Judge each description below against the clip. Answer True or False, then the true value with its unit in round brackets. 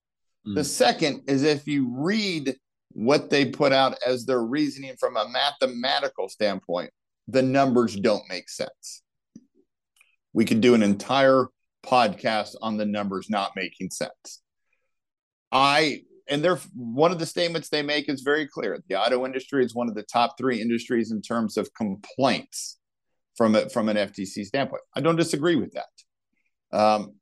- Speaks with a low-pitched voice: True (130 Hz)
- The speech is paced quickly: False (160 wpm)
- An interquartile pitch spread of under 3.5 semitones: False (4.3 semitones)